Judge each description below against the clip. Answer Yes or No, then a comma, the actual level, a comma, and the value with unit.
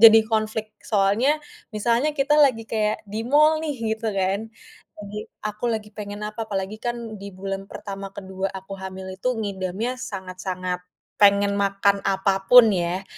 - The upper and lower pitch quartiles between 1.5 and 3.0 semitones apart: Yes, narrow, 2.5 semitones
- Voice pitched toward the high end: Yes, high, 210 Hz